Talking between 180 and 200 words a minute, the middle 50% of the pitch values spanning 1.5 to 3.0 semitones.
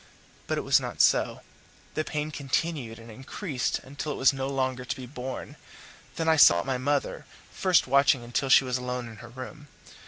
Yes: average, 190 wpm; narrow, 2.6 semitones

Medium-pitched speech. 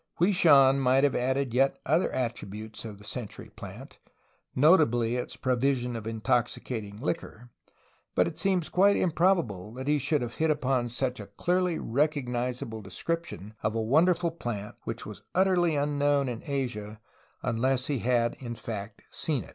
No: low, 130 Hz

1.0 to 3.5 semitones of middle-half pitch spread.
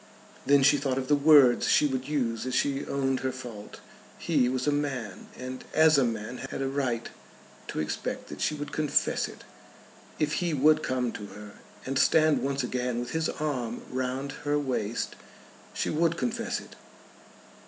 Yes: average, 2.8 semitones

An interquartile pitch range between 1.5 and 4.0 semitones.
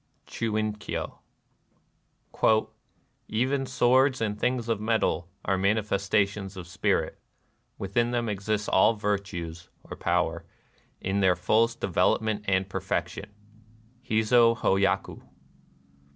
Yes: average, 2.9 semitones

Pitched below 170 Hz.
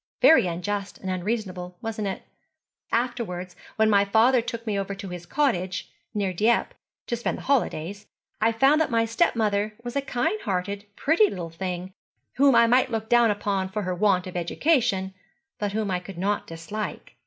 No: high, 205 Hz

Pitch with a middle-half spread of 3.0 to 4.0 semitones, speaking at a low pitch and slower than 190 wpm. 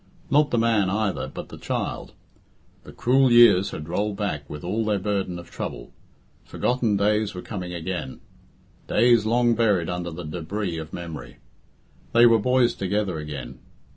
No: average, 4.7 semitones; low, 100 Hz; average, 160 wpm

